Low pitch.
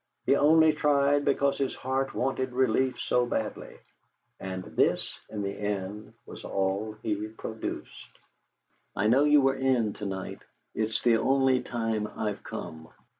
Yes: low, 120 Hz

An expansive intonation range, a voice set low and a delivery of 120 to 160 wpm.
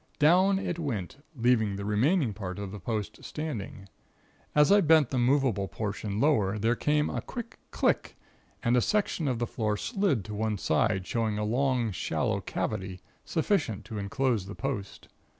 No: wide, 6.2 semitones; low, 115 Hz; average, 170 wpm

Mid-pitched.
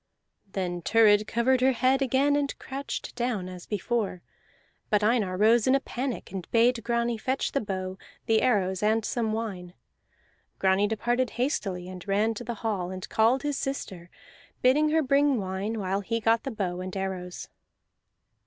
No: high, 220 Hz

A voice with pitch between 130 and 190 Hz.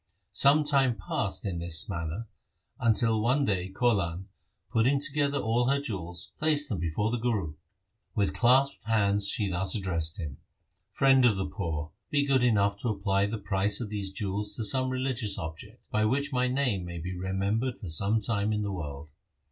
No: low, 105 Hz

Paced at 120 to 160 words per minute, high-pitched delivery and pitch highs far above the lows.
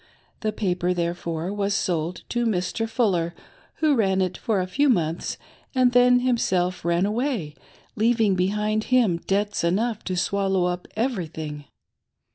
No: average, 145 wpm; high, 195 Hz; average, 4.3 semitones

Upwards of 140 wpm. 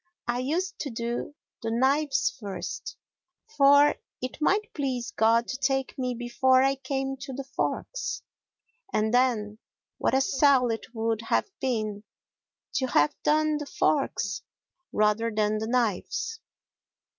No: slow, 135 wpm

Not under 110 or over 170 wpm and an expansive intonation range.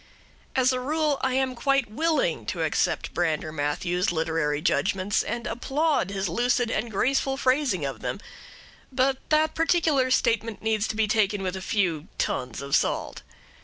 Yes: average, 160 wpm; wide, 6.4 semitones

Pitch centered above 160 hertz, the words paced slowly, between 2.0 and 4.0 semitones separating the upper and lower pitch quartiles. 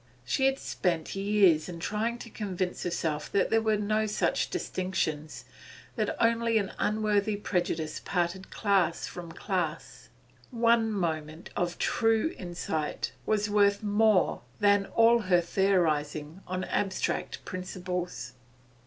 Yes: high, 190 Hz; slow, 125 wpm; average, 3.6 semitones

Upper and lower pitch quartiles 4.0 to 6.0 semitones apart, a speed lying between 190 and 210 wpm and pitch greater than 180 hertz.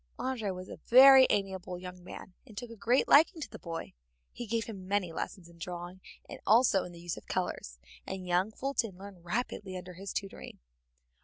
Yes: average, 4.4 semitones; average, 200 wpm; high, 190 Hz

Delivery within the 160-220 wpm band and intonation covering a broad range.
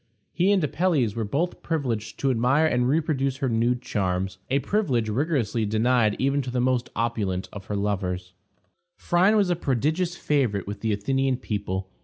Yes: average, 170 wpm; wide, 5.7 semitones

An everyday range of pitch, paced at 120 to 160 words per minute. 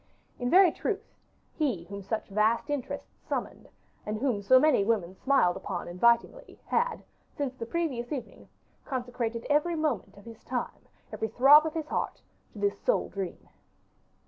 No: wide, 6.0 semitones; average, 155 wpm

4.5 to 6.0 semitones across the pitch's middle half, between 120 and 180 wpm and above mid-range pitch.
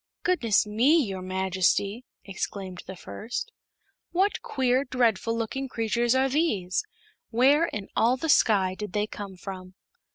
Yes: wide, 5.5 semitones; slow, 135 wpm; high, 225 Hz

